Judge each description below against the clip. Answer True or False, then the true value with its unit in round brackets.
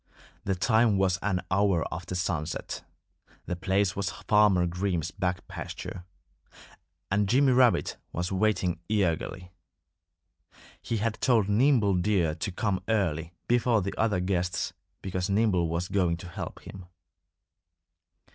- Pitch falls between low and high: False (95 Hz)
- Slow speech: True (130 wpm)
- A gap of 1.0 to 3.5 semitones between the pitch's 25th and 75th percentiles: True (2.9 semitones)